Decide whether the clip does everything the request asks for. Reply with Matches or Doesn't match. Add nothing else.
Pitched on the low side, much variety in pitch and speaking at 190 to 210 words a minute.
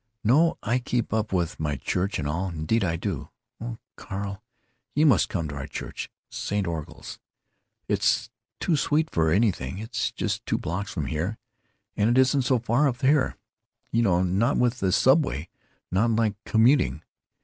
Doesn't match